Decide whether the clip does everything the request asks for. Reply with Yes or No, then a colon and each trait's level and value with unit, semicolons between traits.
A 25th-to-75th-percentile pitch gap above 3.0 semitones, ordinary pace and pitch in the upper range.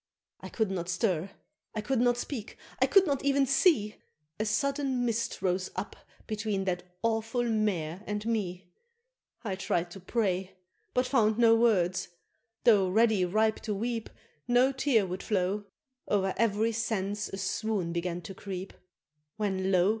Yes: average, 3.6 semitones; average, 155 wpm; high, 210 Hz